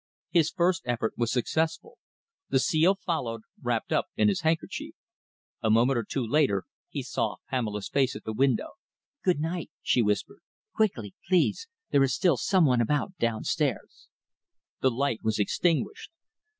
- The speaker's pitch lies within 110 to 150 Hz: Yes, low, 135 Hz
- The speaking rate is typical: Yes, average, 150 wpm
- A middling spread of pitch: No, wide, 6.4 semitones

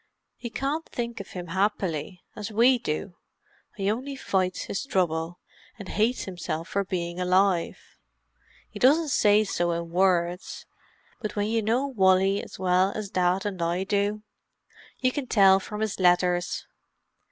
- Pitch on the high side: Yes, high, 195 Hz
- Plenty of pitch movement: No, average, 3.3 semitones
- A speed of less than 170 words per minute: Yes, average, 150 wpm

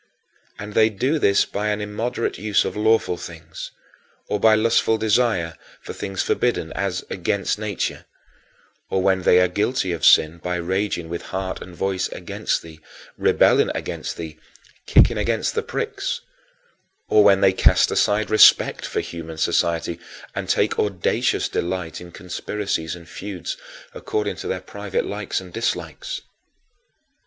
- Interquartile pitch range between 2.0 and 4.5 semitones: Yes, average, 3.8 semitones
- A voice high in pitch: No, low, 100 Hz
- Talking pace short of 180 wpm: Yes, average, 145 wpm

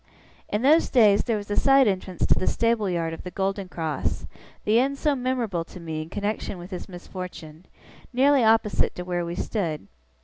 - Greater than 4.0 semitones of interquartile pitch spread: Yes, average, 4.9 semitones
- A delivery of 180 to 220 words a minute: Yes, average, 195 wpm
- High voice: Yes, high, 200 Hz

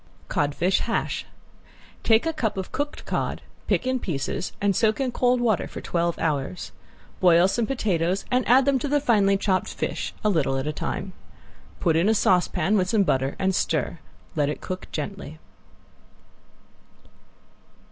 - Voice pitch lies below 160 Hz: No, high, 190 Hz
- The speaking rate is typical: Yes, average, 160 wpm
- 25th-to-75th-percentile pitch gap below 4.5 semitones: No, wide, 5.4 semitones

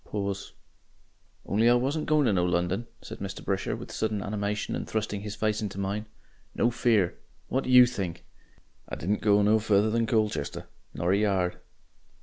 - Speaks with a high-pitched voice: No, low, 105 Hz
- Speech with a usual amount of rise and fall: No, narrow, 2.3 semitones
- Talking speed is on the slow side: No, average, 175 wpm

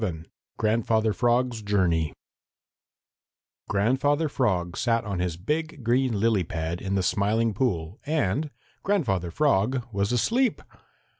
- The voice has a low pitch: Yes, low, 110 Hz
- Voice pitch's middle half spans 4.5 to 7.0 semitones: Yes, wide, 5.4 semitones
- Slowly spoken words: Yes, slow, 120 wpm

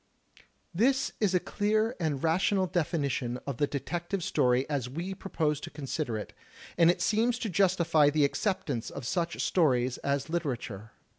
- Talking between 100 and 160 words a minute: Yes, average, 155 wpm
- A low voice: No, medium, 160 Hz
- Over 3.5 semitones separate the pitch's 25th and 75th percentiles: Yes, average, 5.2 semitones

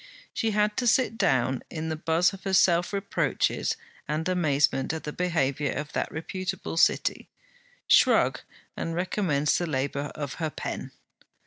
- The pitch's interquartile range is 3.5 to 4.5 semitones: Yes, average, 4.2 semitones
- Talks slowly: No, average, 150 wpm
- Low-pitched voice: No, medium, 165 Hz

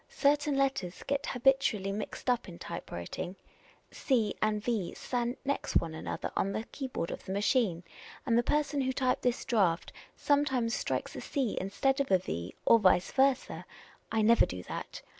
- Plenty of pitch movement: Yes, wide, 5.8 semitones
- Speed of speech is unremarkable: Yes, average, 170 wpm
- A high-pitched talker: Yes, high, 235 Hz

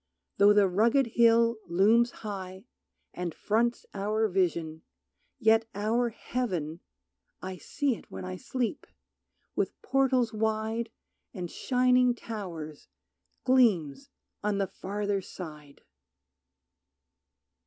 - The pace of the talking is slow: Yes, slow, 100 wpm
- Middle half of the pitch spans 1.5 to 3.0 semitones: No, average, 4.3 semitones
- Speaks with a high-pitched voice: Yes, high, 210 Hz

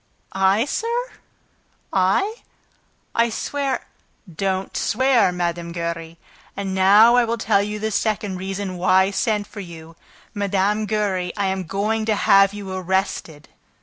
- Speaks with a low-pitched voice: No, high, 200 Hz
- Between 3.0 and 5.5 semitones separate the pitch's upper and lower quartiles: No, narrow, 2.6 semitones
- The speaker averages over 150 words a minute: No, average, 145 wpm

